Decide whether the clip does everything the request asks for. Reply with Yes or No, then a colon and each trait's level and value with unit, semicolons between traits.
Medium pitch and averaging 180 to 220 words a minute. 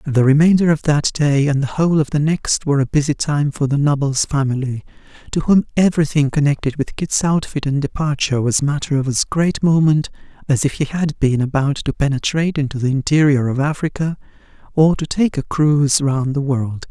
Yes: medium, 145 Hz; average, 195 wpm